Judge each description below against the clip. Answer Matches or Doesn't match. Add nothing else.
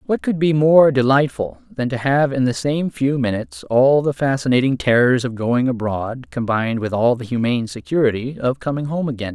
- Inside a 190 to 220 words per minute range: Matches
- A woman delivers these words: Doesn't match